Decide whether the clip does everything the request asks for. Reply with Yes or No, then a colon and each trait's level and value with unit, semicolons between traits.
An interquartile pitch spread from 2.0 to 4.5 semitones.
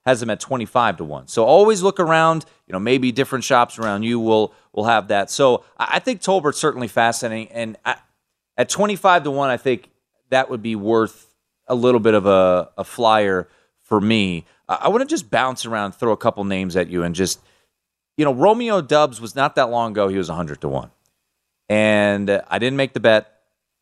No: average, 5.2 semitones